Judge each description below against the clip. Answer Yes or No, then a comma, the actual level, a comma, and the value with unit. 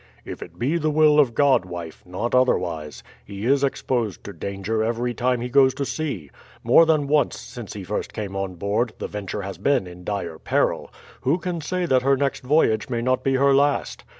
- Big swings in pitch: Yes, wide, 6.0 semitones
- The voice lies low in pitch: Yes, low, 120 Hz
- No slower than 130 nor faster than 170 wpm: No, fast, 205 wpm